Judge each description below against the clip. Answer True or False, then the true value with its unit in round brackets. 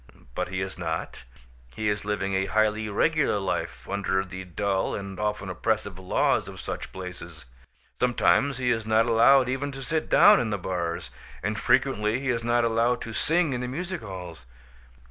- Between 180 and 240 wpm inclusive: True (185 wpm)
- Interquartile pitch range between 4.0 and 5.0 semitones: True (4.5 semitones)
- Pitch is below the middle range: True (105 Hz)